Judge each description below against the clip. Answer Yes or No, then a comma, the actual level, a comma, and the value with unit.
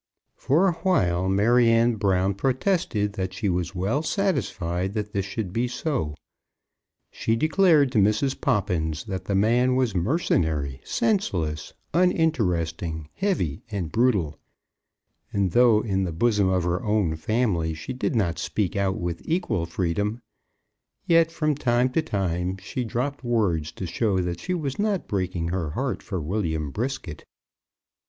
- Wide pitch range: Yes, wide, 6.4 semitones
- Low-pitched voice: Yes, low, 100 Hz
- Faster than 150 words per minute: No, average, 145 wpm